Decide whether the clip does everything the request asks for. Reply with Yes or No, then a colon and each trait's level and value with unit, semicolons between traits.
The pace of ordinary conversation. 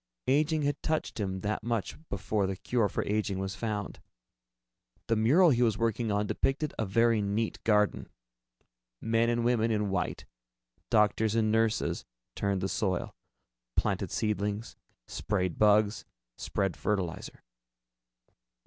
No: slow, 130 wpm